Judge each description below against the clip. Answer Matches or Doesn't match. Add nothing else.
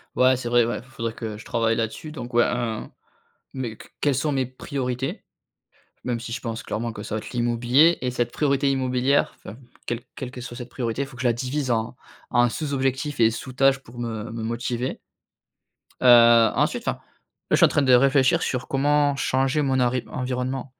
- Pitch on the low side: Matches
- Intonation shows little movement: Matches